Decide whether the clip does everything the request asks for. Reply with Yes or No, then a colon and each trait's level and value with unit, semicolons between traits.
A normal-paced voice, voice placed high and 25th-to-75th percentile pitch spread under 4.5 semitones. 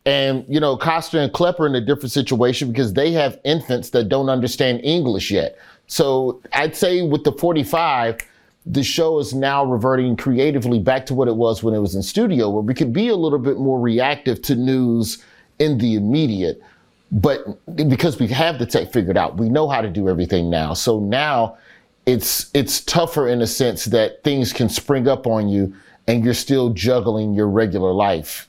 No: average, 195 wpm; low, 130 Hz; average, 3.9 semitones